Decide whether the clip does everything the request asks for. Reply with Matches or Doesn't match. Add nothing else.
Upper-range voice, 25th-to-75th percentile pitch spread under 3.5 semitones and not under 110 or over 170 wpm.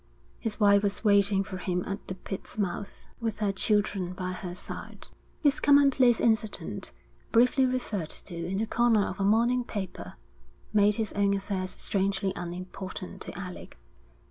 Matches